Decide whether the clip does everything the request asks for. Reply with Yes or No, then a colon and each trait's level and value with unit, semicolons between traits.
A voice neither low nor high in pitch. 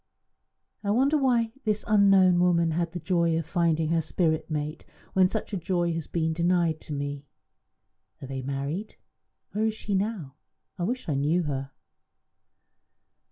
Yes: medium, 170 Hz